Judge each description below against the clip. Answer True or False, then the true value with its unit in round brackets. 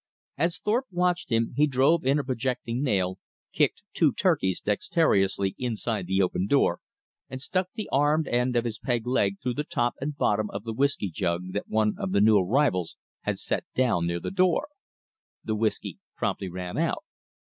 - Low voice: True (120 Hz)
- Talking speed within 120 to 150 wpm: False (180 wpm)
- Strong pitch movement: True (6.7 semitones)